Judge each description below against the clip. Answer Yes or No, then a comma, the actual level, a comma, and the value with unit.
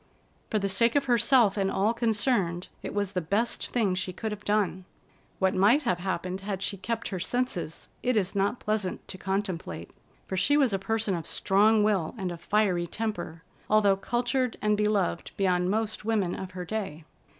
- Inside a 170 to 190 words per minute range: Yes, average, 185 wpm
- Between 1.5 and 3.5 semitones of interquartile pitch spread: Yes, average, 3.1 semitones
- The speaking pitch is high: Yes, high, 200 Hz